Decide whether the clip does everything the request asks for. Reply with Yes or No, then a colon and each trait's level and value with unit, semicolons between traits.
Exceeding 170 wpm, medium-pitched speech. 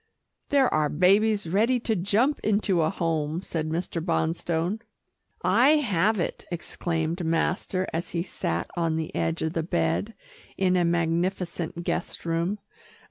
No: average, 140 wpm; medium, 170 Hz